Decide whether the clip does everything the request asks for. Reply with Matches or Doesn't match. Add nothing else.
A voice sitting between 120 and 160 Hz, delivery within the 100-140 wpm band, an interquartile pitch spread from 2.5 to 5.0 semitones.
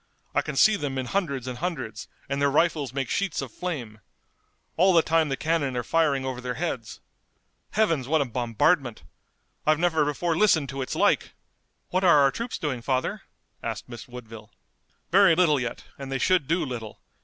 Doesn't match